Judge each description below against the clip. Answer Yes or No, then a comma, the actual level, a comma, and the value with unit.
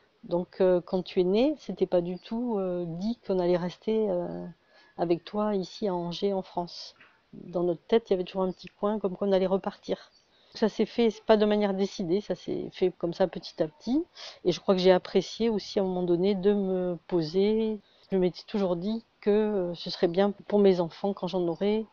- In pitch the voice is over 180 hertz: Yes, high, 190 Hz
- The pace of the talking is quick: Yes, fast, 225 wpm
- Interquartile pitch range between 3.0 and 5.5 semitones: No, narrow, 2.6 semitones